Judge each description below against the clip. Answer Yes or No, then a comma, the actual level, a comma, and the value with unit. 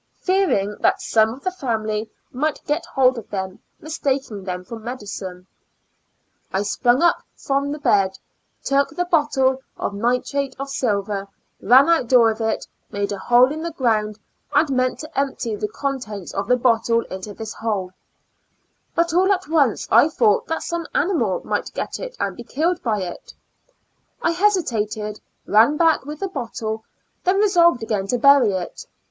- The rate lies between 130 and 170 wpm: Yes, average, 165 wpm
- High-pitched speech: Yes, high, 245 Hz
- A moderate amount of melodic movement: No, wide, 6.1 semitones